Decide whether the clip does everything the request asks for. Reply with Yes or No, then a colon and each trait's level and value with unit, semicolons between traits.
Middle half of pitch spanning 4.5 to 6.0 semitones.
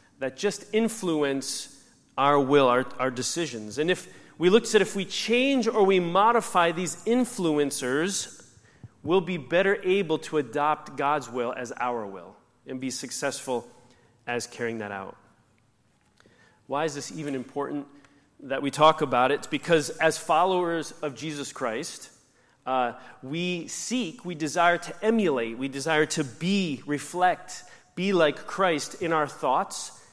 Yes: average, 5.3 semitones